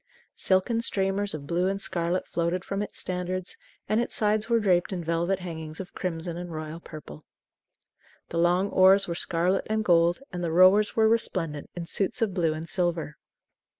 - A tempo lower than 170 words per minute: No, average, 180 wpm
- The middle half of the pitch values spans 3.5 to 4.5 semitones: No, average, 2.7 semitones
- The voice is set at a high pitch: No, medium, 180 Hz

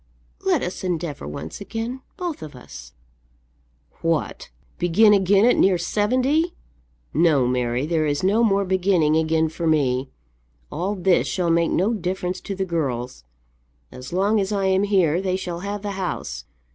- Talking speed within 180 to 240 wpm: No, average, 160 wpm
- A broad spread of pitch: No, average, 4.1 semitones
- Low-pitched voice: No, medium, 185 Hz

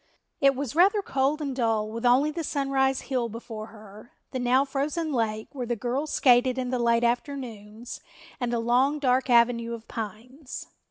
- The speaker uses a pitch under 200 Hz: No, very high, 250 Hz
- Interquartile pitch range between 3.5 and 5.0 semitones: No, average, 2.9 semitones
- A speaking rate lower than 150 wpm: No, average, 175 wpm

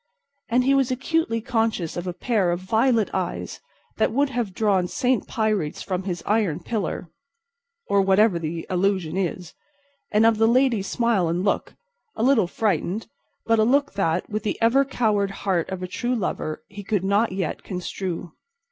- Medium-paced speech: Yes, average, 165 wpm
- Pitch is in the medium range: No, high, 210 Hz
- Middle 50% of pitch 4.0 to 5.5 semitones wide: Yes, average, 5.0 semitones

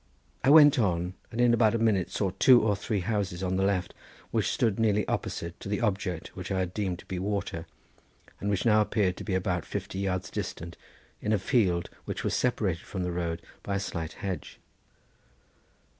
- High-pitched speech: No, very low, 95 Hz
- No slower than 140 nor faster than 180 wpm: No, average, 200 wpm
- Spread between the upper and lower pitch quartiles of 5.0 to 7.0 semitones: No, average, 3.0 semitones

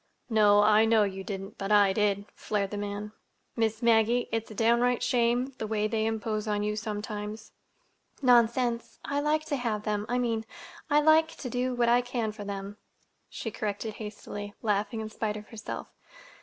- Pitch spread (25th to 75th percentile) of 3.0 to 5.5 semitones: No, narrow, 2.4 semitones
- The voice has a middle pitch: No, high, 220 Hz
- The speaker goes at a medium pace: Yes, average, 170 wpm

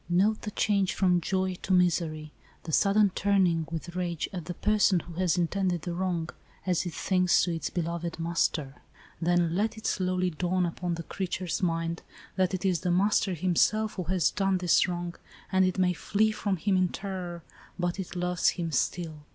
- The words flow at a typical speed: Yes, average, 190 wpm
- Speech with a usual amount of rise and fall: No, narrow, 1.9 semitones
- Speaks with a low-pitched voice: No, medium, 180 Hz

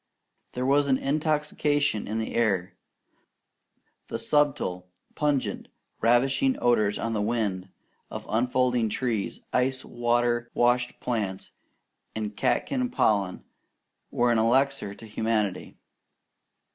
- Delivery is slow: Yes, slow, 105 wpm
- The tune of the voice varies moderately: Yes, average, 3.9 semitones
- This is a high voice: No, low, 120 Hz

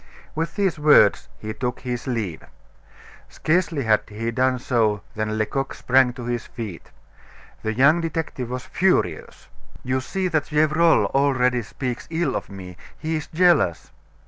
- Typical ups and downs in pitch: No, wide, 5.9 semitones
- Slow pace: No, average, 145 wpm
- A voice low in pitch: Yes, low, 130 Hz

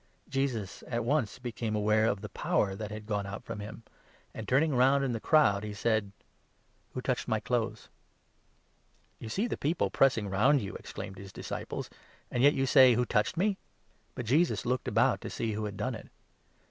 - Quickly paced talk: Yes, fast, 220 wpm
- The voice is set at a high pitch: No, low, 115 Hz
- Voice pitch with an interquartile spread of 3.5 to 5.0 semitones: Yes, average, 4.3 semitones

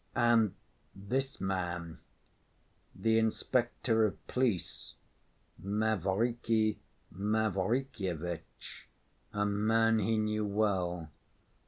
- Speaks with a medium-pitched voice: No, low, 105 Hz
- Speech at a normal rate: No, slow, 65 wpm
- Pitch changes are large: No, average, 2.9 semitones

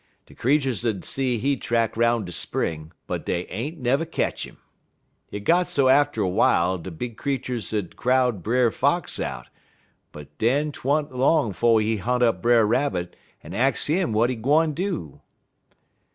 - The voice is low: Yes, low, 120 Hz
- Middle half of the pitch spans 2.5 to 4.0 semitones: No, average, 4.7 semitones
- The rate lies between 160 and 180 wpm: Yes, average, 175 wpm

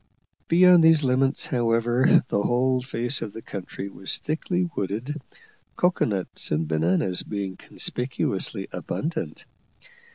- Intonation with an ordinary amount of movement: No, wide, 6.7 semitones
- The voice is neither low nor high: No, low, 120 Hz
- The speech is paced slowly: Yes, slow, 120 wpm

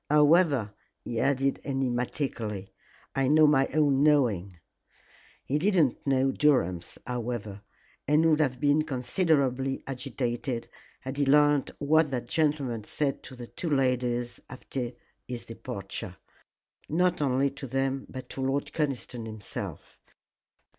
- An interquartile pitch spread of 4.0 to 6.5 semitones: No, average, 3.3 semitones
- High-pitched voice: No, low, 135 Hz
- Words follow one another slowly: Yes, slow, 125 wpm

